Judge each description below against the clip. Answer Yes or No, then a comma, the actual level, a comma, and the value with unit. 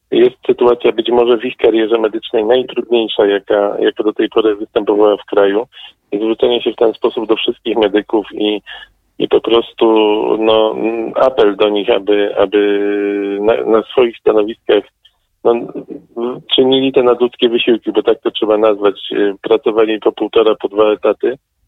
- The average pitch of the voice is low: Yes, low, 115 Hz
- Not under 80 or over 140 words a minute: No, average, 150 wpm